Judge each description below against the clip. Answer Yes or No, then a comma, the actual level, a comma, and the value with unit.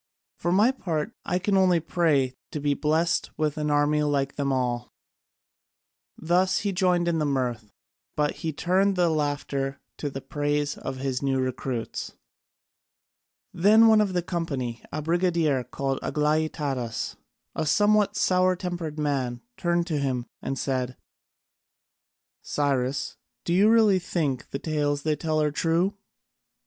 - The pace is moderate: Yes, average, 145 wpm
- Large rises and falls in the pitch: No, average, 4.3 semitones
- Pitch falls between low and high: Yes, medium, 150 Hz